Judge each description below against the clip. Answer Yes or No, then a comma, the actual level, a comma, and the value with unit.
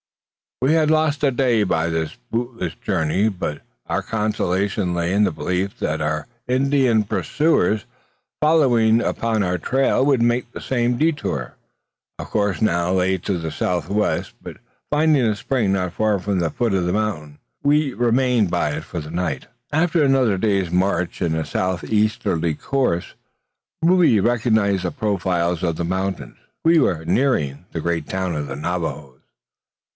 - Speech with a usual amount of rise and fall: No, wide, 6.0 semitones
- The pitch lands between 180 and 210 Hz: No, low, 100 Hz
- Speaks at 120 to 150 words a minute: No, average, 160 wpm